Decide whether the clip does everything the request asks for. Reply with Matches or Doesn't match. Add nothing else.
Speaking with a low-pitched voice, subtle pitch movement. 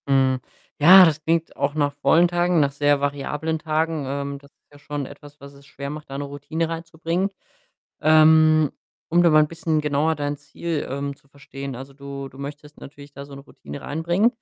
Doesn't match